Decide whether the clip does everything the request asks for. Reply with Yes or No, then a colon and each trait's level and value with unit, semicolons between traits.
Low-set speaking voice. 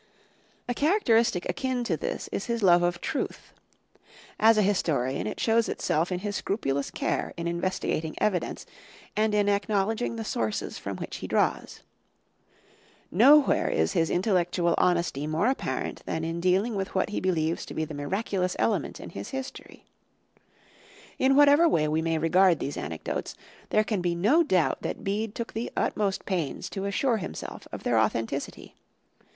No: high, 190 Hz